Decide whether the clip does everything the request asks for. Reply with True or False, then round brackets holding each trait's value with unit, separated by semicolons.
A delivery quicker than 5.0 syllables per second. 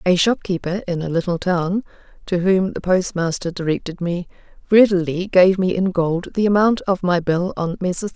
False (4.8 syllables/s)